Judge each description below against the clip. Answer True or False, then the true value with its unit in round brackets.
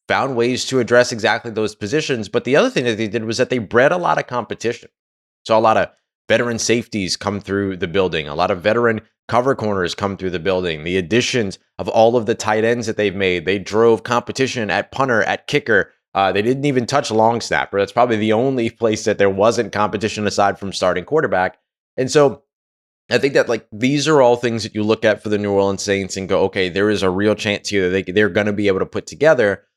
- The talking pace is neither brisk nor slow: False (235 wpm)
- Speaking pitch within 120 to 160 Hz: False (110 Hz)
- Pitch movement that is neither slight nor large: True (3.2 semitones)